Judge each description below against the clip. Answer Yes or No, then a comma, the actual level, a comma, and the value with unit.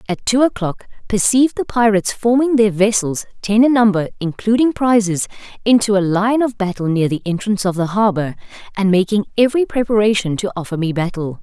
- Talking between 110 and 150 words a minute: No, average, 175 wpm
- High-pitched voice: Yes, high, 210 Hz